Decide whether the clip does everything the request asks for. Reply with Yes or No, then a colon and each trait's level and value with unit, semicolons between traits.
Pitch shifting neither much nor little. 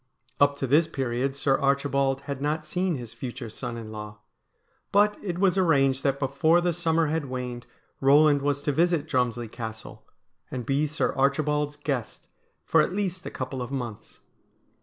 Yes: average, 3.5 semitones